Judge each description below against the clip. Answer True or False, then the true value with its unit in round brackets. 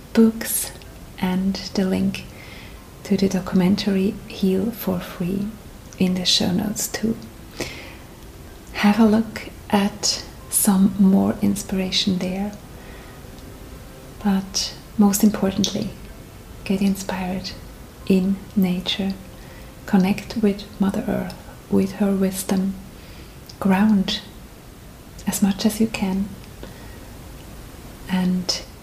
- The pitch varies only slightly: True (1.6 semitones)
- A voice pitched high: True (195 Hz)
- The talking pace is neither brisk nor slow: False (90 wpm)